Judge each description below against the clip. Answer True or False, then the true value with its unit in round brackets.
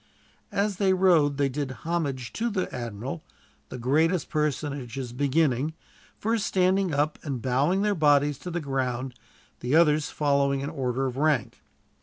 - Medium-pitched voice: True (145 Hz)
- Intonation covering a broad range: False (4.2 semitones)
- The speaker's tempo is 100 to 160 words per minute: True (150 wpm)